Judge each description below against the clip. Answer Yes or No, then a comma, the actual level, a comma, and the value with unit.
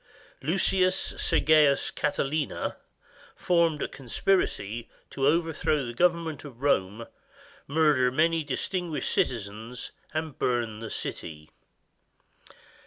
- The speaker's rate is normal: No, slow, 95 wpm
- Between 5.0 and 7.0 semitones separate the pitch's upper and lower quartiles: Yes, average, 5.3 semitones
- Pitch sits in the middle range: Yes, medium, 145 Hz